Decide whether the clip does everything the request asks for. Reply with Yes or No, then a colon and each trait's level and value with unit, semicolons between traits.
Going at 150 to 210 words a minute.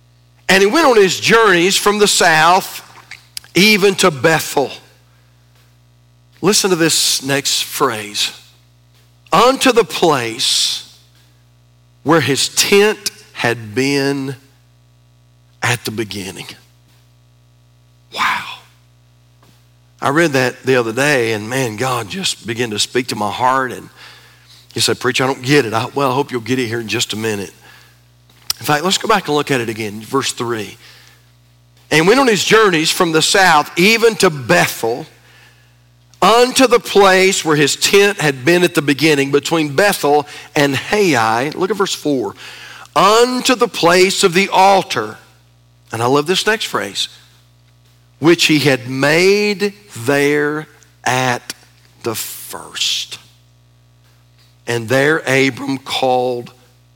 No: average, 140 wpm